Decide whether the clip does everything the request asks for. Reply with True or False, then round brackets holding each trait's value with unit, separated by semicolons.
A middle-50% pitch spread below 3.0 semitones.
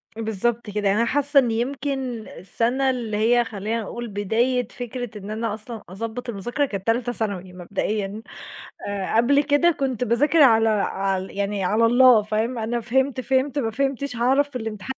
False (3.4 semitones)